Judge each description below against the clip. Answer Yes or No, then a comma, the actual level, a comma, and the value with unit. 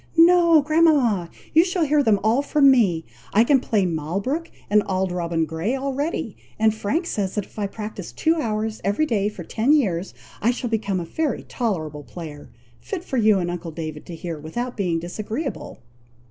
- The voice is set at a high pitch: Yes, high, 215 Hz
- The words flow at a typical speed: Yes, average, 180 wpm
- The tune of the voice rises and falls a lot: Yes, wide, 7.8 semitones